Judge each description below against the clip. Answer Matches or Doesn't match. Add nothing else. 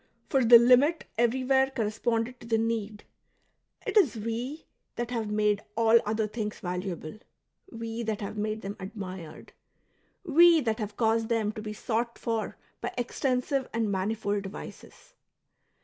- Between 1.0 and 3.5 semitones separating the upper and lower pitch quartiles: Matches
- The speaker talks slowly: Doesn't match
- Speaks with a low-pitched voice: Doesn't match